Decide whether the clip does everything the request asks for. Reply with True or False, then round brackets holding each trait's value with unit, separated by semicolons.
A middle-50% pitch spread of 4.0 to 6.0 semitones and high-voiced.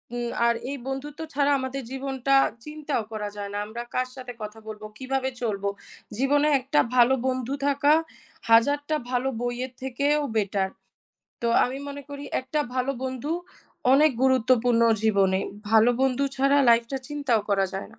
False (3.2 semitones; 260 Hz)